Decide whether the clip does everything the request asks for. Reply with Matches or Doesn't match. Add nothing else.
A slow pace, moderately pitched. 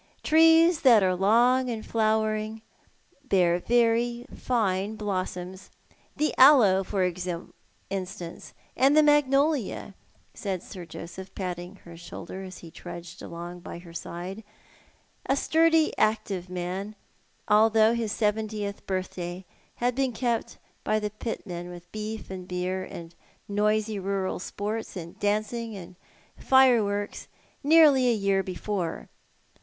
Doesn't match